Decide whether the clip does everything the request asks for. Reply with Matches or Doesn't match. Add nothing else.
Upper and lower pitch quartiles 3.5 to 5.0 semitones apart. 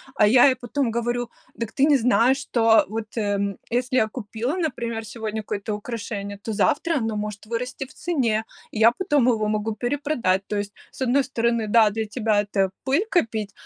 Doesn't match